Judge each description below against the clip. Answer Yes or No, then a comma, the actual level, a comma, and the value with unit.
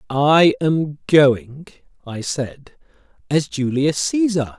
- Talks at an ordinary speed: No, slow, 105 wpm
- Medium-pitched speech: Yes, medium, 150 Hz